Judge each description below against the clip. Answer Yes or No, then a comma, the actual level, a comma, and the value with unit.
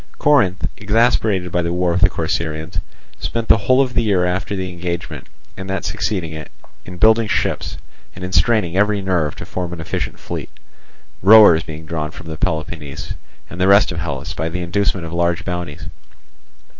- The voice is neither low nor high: No, very low, 90 Hz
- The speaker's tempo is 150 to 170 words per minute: No, average, 180 wpm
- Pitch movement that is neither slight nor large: Yes, average, 3.3 semitones